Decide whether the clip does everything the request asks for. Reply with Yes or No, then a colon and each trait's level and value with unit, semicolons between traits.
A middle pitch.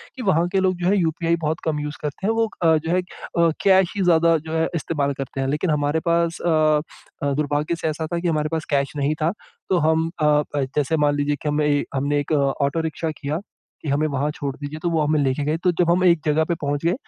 Yes: medium, 155 Hz